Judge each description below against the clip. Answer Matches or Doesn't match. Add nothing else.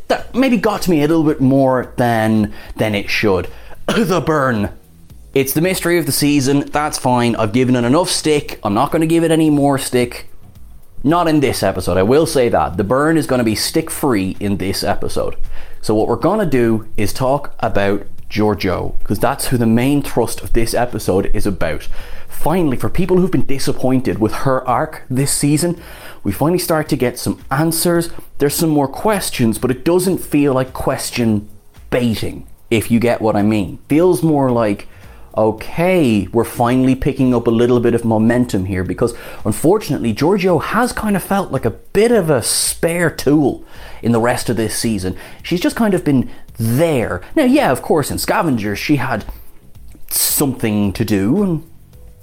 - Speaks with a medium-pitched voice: Doesn't match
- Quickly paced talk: Doesn't match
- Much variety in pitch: Matches